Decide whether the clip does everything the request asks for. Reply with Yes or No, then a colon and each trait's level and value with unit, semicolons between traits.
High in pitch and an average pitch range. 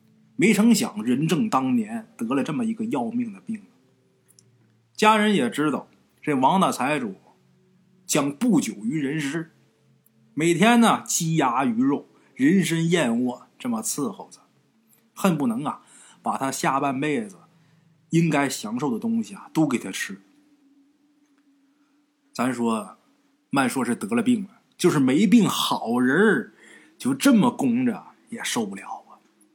No: high, 225 Hz; wide, 7.3 semitones